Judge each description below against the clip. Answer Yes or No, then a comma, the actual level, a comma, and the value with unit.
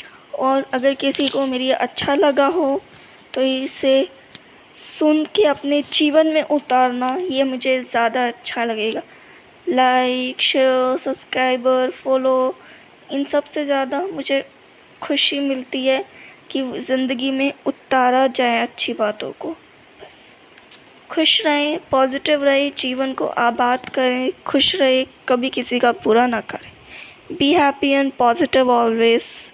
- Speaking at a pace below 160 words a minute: Yes, average, 130 wpm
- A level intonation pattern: Yes, narrow, 2.1 semitones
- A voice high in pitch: Yes, very high, 265 Hz